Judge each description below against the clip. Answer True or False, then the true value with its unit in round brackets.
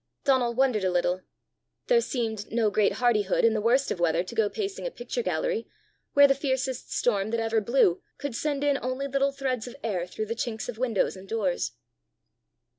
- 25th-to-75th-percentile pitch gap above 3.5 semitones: True (4.4 semitones)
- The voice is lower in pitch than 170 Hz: False (235 Hz)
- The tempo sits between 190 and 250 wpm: True (195 wpm)